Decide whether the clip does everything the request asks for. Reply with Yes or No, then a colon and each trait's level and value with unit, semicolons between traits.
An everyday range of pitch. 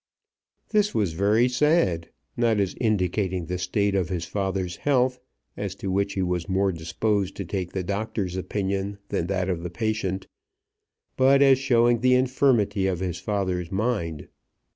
Yes: average, 4.1 semitones